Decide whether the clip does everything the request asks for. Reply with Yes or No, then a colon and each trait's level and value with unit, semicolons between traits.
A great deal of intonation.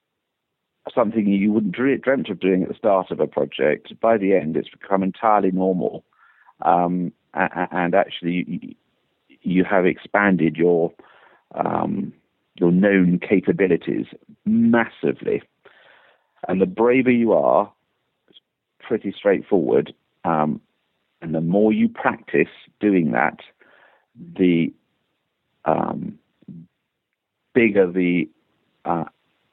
No: average, 3.3 semitones